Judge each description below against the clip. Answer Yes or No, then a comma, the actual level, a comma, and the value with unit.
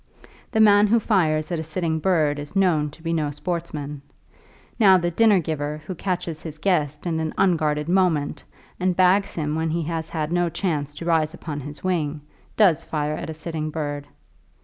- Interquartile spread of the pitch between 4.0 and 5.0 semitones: No, average, 3.1 semitones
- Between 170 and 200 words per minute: Yes, average, 190 wpm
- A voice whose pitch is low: No, medium, 160 Hz